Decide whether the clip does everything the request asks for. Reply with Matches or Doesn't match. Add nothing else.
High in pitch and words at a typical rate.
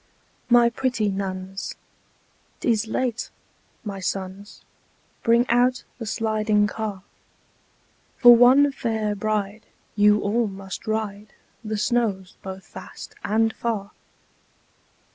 Doesn't match